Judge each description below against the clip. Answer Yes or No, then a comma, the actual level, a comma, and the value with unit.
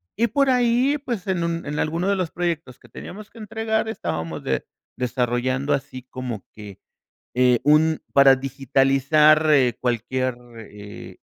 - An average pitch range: No, wide, 6.7 semitones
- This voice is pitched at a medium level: Yes, medium, 145 Hz